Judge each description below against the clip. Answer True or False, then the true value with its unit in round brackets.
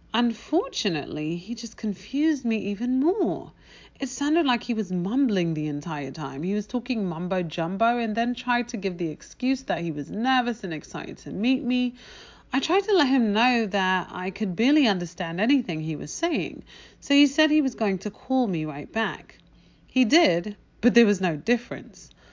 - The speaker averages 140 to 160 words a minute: False (190 wpm)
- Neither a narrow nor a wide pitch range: False (5.9 semitones)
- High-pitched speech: True (230 Hz)